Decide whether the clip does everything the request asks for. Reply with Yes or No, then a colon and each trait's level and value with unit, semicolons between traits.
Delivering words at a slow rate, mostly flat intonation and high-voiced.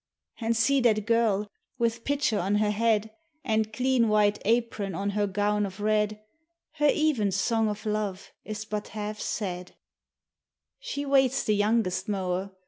No: average, 155 wpm; narrow, 2.1 semitones; high, 215 Hz